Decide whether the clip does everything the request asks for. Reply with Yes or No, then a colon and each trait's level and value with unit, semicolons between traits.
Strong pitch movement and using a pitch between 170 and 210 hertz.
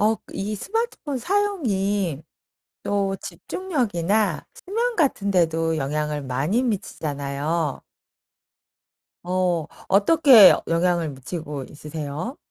Yes: wide, 7.3 semitones; medium, 185 Hz